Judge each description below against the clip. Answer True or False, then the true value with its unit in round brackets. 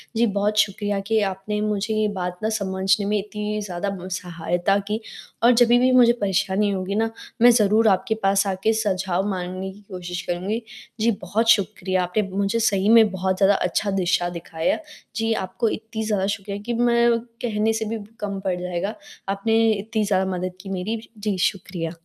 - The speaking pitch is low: False (200 Hz)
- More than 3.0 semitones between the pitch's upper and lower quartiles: False (2.6 semitones)